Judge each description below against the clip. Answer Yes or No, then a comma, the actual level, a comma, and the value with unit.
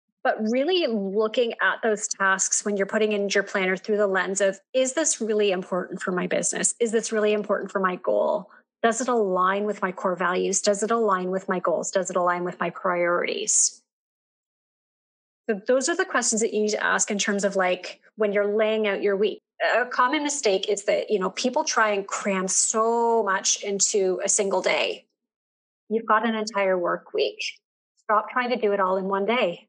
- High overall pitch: Yes, high, 210 Hz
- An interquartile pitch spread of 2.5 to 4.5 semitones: Yes, average, 3.0 semitones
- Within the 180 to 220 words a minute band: Yes, fast, 205 wpm